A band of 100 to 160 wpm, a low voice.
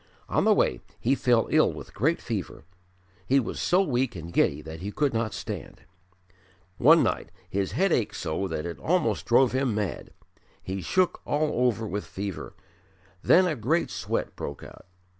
No: average, 175 wpm; low, 115 Hz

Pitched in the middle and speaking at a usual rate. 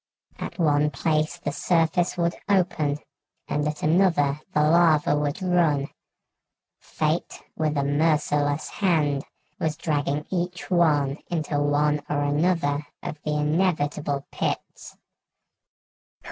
No: medium, 150 Hz; slow, 115 wpm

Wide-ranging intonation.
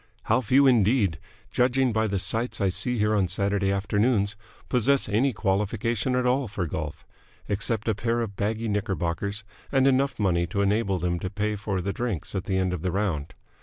No: average, 3.4 semitones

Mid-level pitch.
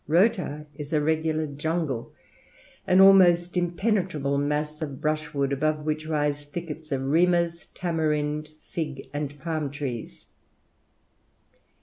Yes: medium, 155 Hz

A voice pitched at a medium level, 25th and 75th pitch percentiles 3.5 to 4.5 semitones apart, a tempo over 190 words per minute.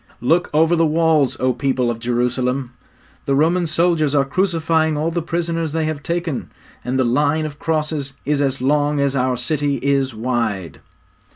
No: medium, 145 Hz; average, 3.8 semitones; average, 170 wpm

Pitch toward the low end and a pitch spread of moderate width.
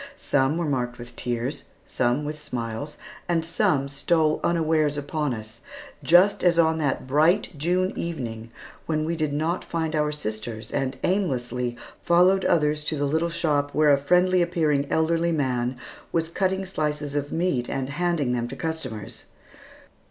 No: medium, 150 Hz; average, 4.1 semitones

